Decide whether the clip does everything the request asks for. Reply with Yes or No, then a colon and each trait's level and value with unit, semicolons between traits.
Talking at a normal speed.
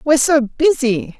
Yes: average, 150 wpm